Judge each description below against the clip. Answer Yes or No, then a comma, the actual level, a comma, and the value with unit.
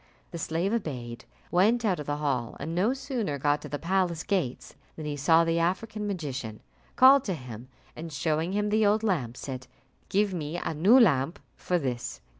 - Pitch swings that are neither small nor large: No, wide, 6.1 semitones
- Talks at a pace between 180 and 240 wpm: Yes, average, 190 wpm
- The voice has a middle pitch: Yes, medium, 165 Hz